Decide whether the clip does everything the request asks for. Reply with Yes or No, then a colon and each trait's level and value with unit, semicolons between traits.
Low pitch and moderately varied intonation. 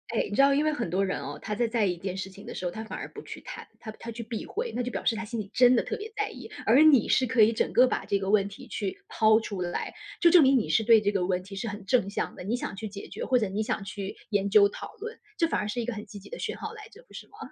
No: high, 220 Hz; average, 3.9 semitones